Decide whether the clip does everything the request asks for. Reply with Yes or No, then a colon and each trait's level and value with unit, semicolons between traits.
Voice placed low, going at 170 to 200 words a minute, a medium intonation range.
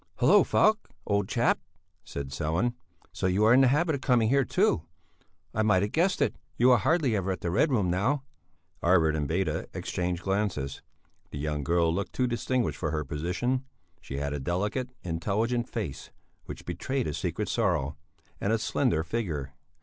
No: low, 100 Hz; average, 180 wpm; wide, 7.2 semitones